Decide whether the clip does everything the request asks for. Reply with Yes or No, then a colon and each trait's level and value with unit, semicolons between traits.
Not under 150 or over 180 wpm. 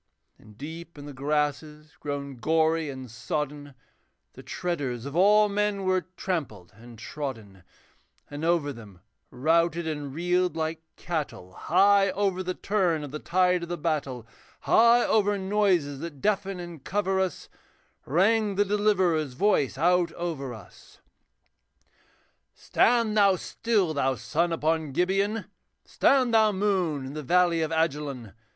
No: average, 140 wpm